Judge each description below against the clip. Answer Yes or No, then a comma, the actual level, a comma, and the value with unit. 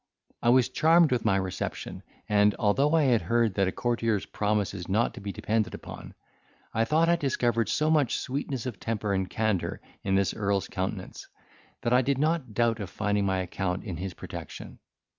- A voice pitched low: Yes, low, 110 Hz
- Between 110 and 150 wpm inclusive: No, average, 190 wpm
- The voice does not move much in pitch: No, average, 4.4 semitones